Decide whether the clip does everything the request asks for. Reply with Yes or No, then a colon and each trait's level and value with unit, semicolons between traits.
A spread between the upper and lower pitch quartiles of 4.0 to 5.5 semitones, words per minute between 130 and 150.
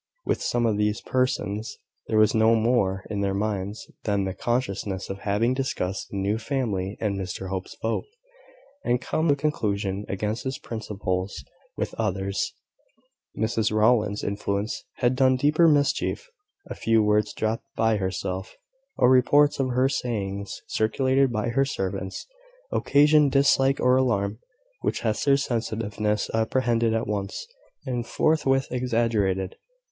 Yes: average, 4.3 semitones; average, 140 wpm